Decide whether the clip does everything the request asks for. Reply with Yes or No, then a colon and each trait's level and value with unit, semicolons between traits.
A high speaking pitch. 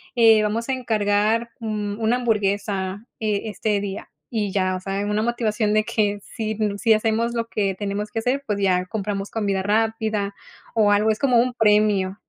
Yes: high, 210 Hz